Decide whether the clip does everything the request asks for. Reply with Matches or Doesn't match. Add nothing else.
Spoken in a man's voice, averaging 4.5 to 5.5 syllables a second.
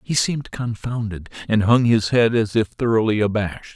Matches